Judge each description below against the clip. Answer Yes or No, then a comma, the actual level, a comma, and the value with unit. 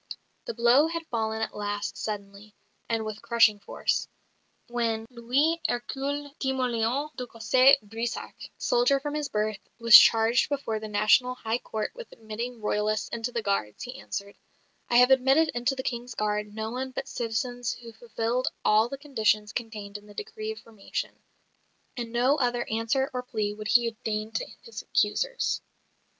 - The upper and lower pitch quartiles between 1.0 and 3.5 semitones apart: Yes, average, 3.1 semitones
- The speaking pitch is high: Yes, high, 235 Hz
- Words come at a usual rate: Yes, average, 165 wpm